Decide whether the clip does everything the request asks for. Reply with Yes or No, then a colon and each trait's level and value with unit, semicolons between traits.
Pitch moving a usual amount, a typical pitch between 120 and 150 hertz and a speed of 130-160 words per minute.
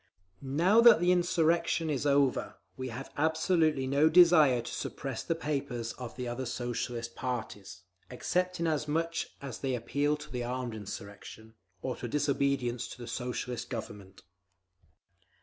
Yes: average, 4.6 semitones; low, 135 Hz; slow, 135 wpm